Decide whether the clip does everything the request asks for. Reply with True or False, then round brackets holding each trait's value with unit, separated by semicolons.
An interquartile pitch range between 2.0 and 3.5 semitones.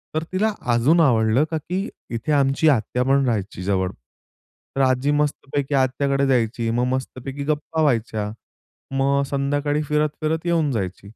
False (3.9 semitones)